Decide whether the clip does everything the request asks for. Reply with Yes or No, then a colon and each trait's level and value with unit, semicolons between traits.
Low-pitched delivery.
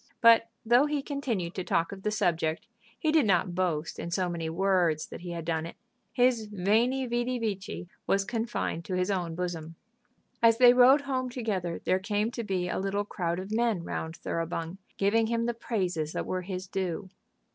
No: high, 195 Hz